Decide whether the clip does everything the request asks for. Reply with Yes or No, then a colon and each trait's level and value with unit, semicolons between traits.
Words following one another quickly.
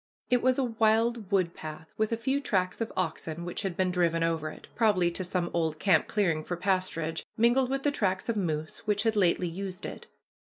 Yes: fast, 215 wpm